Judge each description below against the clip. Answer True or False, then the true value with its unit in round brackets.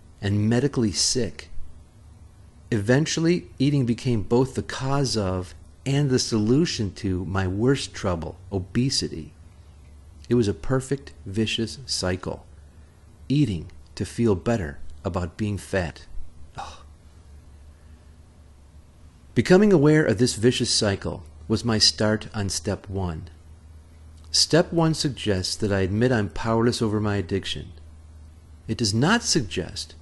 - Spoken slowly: True (120 wpm)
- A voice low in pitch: True (95 Hz)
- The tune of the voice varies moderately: False (6.6 semitones)